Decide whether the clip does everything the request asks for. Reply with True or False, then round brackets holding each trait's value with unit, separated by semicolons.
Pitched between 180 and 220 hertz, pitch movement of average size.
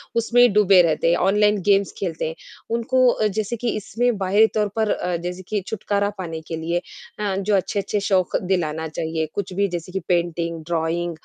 True (190 Hz; 3.5 semitones)